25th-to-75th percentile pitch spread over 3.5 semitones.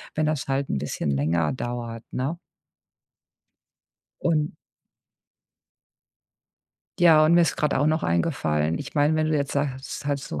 Yes: average, 5.2 semitones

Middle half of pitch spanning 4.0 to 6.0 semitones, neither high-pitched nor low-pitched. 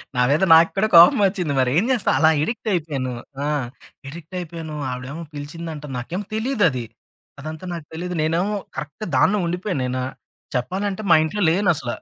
Yes: average, 4.6 semitones; medium, 165 Hz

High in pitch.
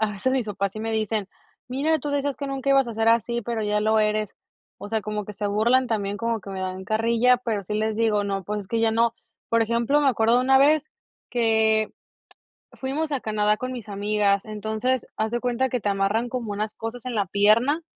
Yes: high, 225 Hz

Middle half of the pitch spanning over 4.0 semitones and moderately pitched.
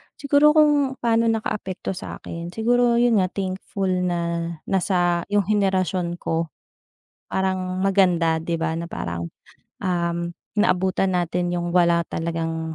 No: average, 3.0 semitones; medium, 180 Hz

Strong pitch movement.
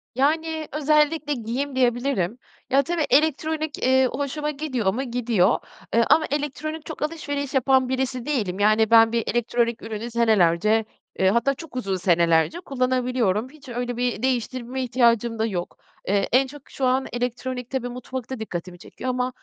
No: average, 3.6 semitones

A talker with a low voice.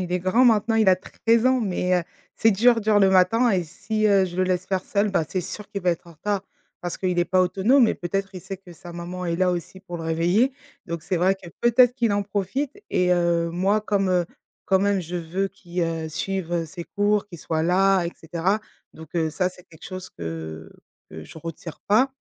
No: medium, 185 Hz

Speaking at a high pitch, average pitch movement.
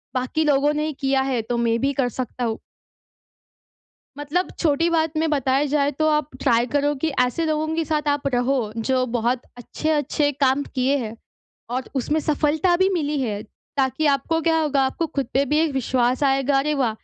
Yes: very high, 280 Hz; average, 3.0 semitones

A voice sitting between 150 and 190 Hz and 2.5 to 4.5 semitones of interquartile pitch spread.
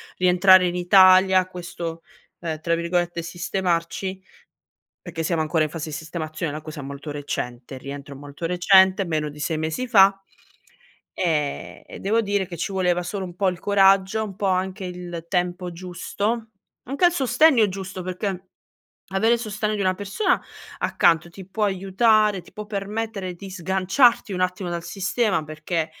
Yes: medium, 185 Hz; average, 2.9 semitones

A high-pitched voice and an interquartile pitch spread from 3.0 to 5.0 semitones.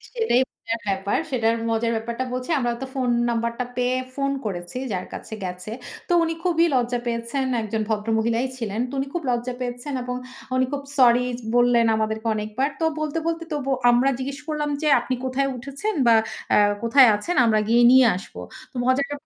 Yes: high, 245 Hz; average, 3.3 semitones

